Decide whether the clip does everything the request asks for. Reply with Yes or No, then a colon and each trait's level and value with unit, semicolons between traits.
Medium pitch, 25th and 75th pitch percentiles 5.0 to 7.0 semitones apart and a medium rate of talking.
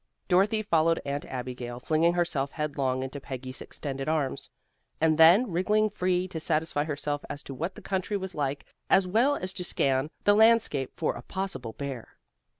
Yes: medium, 160 Hz; average, 5.3 semitones; average, 170 wpm